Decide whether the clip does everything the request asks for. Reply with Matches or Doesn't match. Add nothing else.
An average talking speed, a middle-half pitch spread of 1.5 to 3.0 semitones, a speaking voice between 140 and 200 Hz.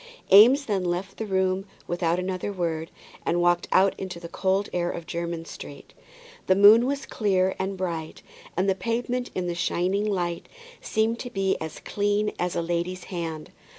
Matches